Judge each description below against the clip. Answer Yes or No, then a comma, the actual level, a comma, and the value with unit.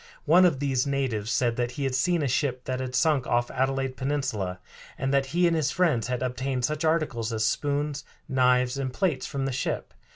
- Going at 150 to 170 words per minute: No, fast, 205 wpm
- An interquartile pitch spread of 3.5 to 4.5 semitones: No, narrow, 2.5 semitones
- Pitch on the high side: No, low, 135 Hz